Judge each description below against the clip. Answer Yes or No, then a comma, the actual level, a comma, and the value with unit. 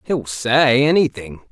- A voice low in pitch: Yes, low, 130 Hz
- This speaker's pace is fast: No, slow, 120 wpm